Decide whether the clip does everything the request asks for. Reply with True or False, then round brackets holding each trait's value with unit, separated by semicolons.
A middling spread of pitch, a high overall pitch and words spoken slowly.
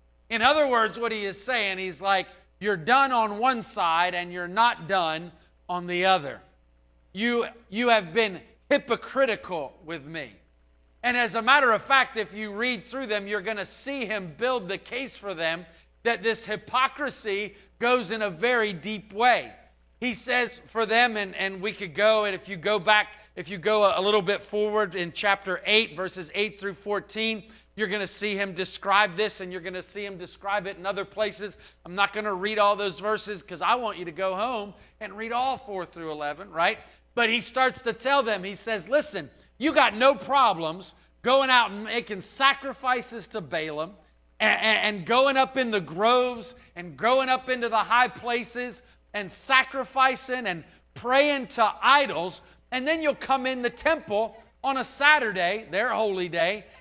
False (4.2 semitones; 210 Hz; 185 wpm)